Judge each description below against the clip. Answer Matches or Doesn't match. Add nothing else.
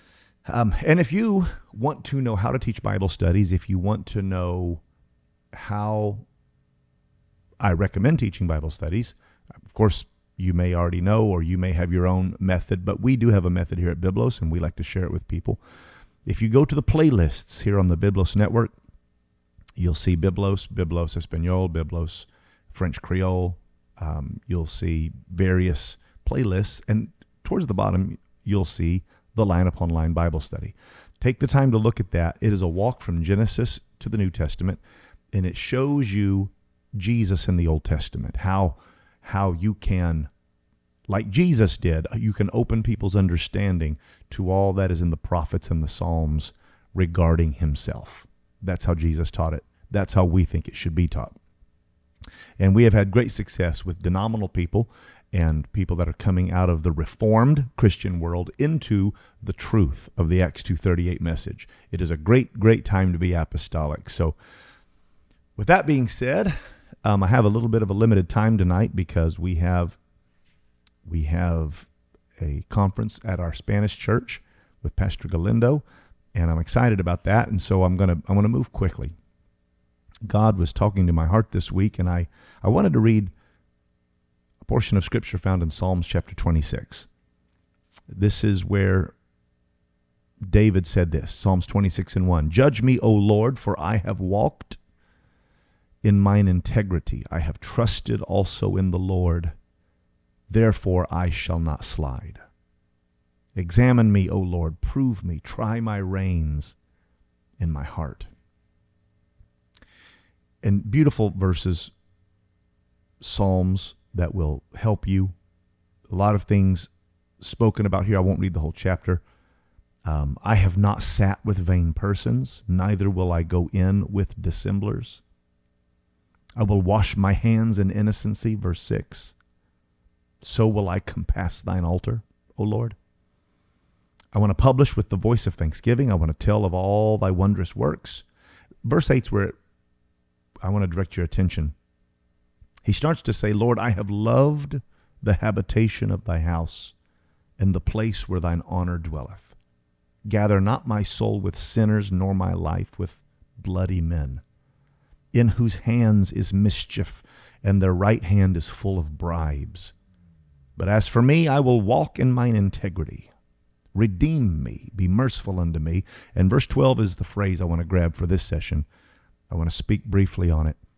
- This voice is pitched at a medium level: Doesn't match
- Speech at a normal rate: Matches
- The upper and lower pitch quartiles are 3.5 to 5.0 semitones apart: Matches